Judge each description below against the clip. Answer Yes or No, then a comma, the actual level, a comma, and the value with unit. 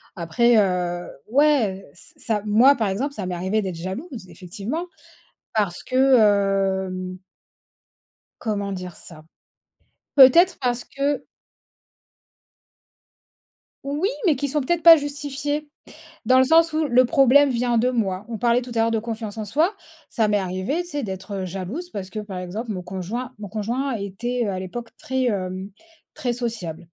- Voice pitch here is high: Yes, high, 225 Hz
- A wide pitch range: Yes, wide, 6.0 semitones